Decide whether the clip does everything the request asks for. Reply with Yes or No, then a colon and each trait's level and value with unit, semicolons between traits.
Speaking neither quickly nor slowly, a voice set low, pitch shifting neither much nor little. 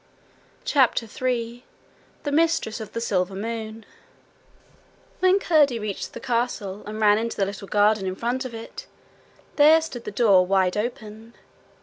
No: average, 145 wpm; high, 225 Hz; average, 3.3 semitones